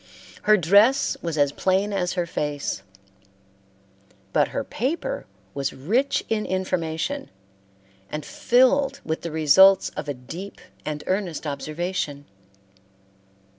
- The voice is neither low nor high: Yes, medium, 180 Hz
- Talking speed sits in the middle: No, slow, 115 wpm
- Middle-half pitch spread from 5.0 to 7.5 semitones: Yes, wide, 5.6 semitones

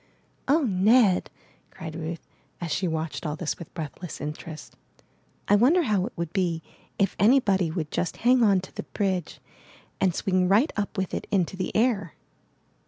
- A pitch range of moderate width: Yes, average, 3.9 semitones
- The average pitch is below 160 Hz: No, medium, 185 Hz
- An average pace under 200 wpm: Yes, average, 170 wpm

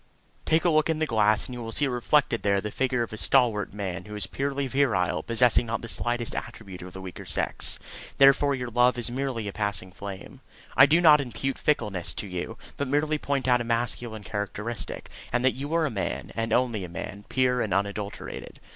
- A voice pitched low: Yes, low, 120 Hz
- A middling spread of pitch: Yes, average, 4.7 semitones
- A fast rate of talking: Yes, fast, 210 wpm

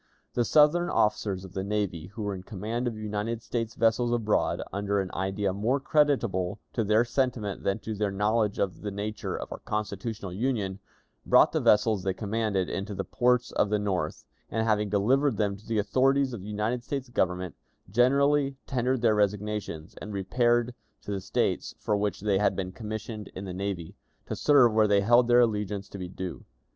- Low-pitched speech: Yes, low, 105 Hz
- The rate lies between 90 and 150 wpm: No, average, 190 wpm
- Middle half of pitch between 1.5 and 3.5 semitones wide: Yes, average, 3.2 semitones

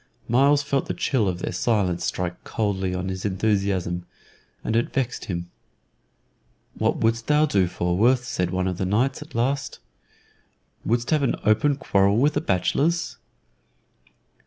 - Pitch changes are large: Yes, wide, 6.4 semitones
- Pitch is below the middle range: Yes, low, 110 Hz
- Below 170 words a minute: Yes, average, 155 wpm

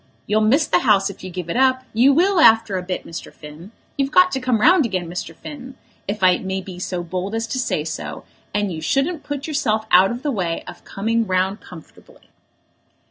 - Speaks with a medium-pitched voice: No, high, 215 Hz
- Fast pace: Yes, fast, 215 wpm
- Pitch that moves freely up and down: Yes, wide, 6.3 semitones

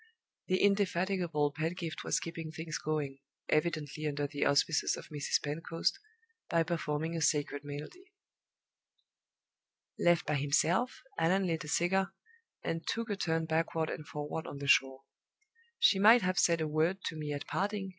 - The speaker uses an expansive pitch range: No, average, 3.3 semitones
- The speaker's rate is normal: Yes, average, 155 wpm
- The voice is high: No, medium, 160 Hz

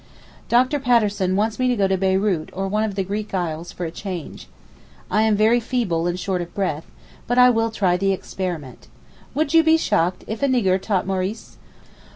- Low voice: No, high, 200 Hz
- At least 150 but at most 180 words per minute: No, average, 195 wpm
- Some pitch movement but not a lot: Yes, average, 3.7 semitones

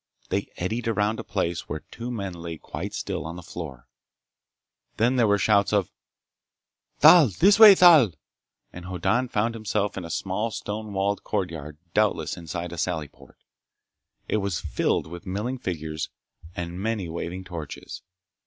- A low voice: Yes, very low, 95 Hz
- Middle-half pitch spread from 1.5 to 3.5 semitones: No, average, 4.3 semitones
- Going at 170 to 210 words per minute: No, average, 155 wpm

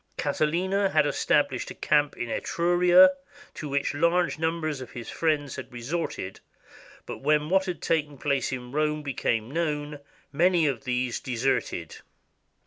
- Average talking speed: Yes, average, 145 wpm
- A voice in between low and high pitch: Yes, medium, 150 Hz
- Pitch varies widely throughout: No, average, 3.7 semitones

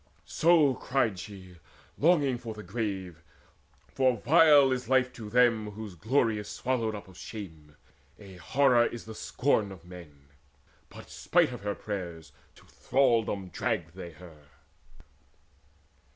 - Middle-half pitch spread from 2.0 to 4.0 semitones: No, wide, 5.6 semitones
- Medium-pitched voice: No, low, 105 Hz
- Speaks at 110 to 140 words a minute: Yes, slow, 135 wpm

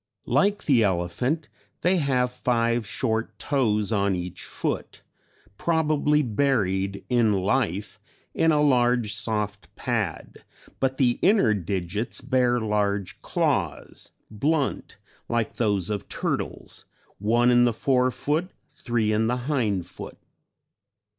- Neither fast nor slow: No, slow, 120 wpm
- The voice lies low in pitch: Yes, low, 120 Hz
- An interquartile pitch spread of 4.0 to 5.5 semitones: Yes, average, 4.3 semitones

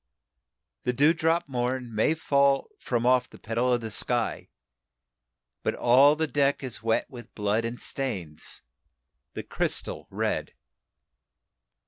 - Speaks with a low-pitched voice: Yes, low, 125 Hz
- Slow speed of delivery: Yes, slow, 125 wpm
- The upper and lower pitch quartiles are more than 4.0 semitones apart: No, average, 3.3 semitones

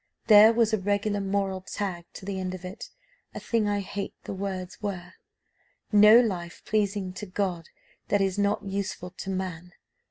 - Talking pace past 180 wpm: No, average, 170 wpm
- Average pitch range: No, narrow, 1.8 semitones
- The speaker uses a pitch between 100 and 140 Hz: No, high, 195 Hz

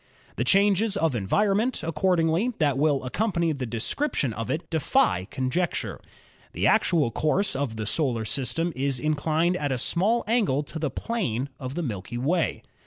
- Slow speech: No, average, 160 wpm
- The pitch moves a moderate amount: No, wide, 6.1 semitones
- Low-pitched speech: No, medium, 155 Hz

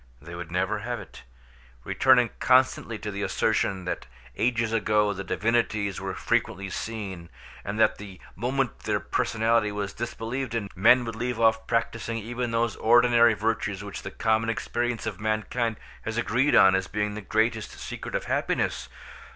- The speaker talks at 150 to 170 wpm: Yes, average, 160 wpm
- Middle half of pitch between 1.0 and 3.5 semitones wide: Yes, narrow, 2.4 semitones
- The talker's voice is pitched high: No, low, 110 Hz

